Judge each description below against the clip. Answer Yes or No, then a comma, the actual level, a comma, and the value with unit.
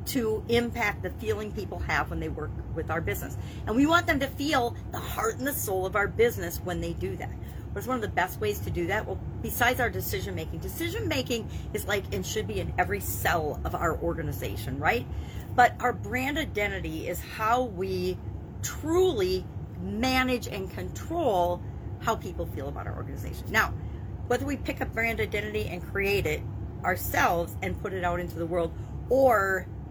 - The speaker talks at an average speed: Yes, average, 190 wpm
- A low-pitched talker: Yes, low, 110 Hz